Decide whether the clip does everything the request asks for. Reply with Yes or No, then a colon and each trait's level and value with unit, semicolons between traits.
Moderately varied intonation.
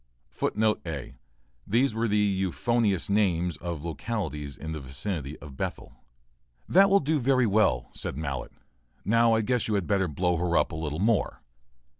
No: wide, 6.2 semitones